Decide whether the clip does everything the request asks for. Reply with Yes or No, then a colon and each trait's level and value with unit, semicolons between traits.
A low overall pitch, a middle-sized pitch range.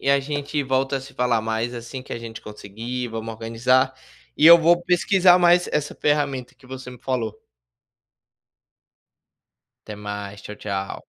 Yes: low, 125 Hz; average, 4.3 semitones